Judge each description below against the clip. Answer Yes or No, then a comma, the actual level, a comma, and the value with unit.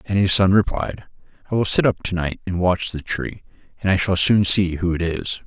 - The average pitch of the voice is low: Yes, very low, 95 Hz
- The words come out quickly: Yes, fast, 240 wpm